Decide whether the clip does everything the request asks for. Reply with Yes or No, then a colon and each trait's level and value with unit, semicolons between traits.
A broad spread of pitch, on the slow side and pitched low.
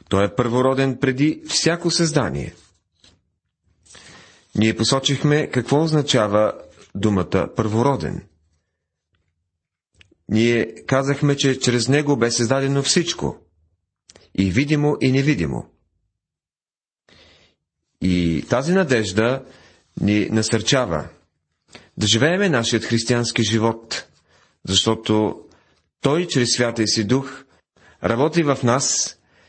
Yes: wide, 6.6 semitones; slow, 90 wpm; low, 115 Hz